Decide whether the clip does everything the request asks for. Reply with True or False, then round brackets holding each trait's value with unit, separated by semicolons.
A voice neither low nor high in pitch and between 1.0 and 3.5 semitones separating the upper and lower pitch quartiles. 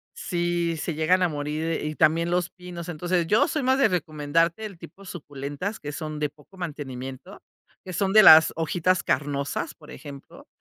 True (165 Hz; 3.2 semitones)